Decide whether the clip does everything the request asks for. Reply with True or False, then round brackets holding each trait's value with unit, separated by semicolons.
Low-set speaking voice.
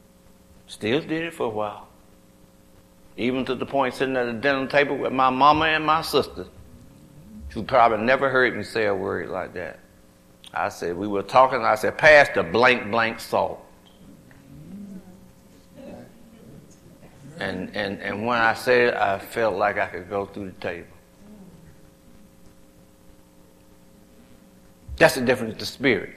True (105 Hz)